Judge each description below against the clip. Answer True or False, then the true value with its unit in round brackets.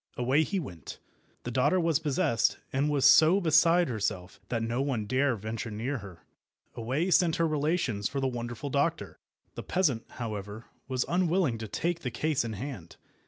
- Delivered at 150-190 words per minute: True (170 wpm)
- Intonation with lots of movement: True (5.7 semitones)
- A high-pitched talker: False (130 Hz)